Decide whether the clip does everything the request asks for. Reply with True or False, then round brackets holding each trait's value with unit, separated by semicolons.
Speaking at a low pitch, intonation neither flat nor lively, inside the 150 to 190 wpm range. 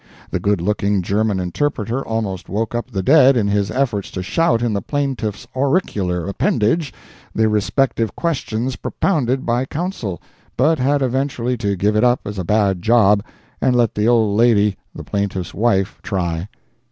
True (110 Hz; 4.2 semitones; 165 wpm)